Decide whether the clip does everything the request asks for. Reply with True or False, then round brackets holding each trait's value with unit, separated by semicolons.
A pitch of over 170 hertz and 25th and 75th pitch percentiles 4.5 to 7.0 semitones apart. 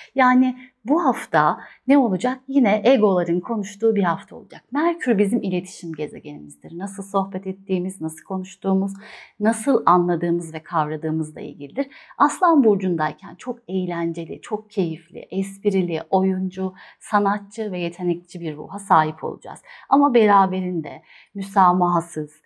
True (190 Hz; 4.9 semitones)